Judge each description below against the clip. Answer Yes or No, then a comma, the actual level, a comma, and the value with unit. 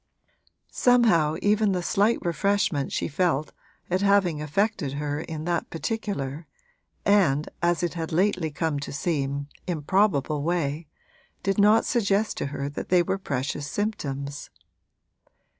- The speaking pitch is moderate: Yes, medium, 170 Hz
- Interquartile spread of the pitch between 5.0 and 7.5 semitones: Yes, wide, 5.4 semitones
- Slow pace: Yes, slow, 130 wpm